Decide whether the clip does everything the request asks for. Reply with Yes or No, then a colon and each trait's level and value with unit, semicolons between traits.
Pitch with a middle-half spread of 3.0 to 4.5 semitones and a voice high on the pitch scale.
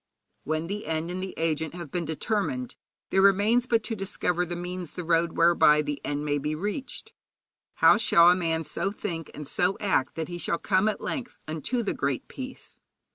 No: average, 4.1 semitones; medium, 175 Hz